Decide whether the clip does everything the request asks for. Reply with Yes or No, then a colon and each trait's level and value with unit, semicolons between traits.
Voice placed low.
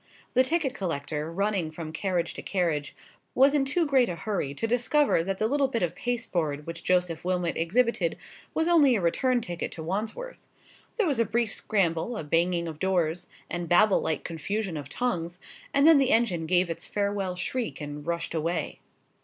No: medium, 185 Hz